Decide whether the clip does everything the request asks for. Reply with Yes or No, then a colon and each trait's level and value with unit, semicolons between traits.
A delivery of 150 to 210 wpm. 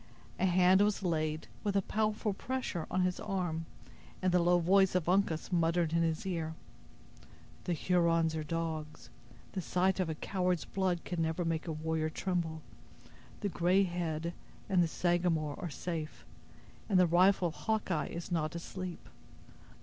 Yes: average, 160 wpm